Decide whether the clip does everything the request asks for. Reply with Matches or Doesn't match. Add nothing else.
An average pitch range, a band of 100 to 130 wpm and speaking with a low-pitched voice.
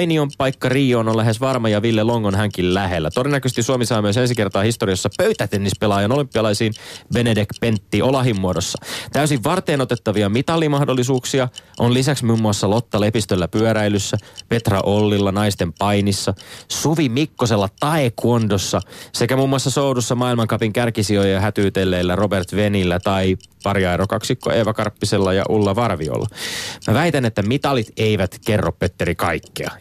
Doesn't match